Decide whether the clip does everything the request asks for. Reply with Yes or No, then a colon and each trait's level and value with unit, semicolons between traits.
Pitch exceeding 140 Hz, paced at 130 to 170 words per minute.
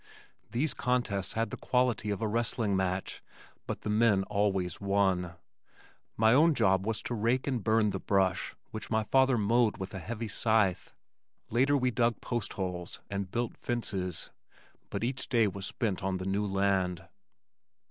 No: low, 105 Hz; average, 160 wpm